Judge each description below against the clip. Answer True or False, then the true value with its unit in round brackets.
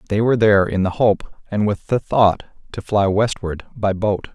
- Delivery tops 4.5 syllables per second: True (5.1 syllables/s)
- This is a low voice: True (105 Hz)